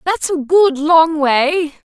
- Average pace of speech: Yes, average, 160 wpm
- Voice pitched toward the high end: Yes, very high, 315 Hz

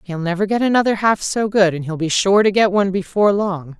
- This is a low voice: No, high, 195 Hz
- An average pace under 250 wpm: No, fast, 255 wpm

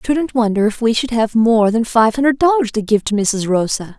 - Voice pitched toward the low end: No, high, 230 Hz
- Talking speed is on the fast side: Yes, fast, 255 wpm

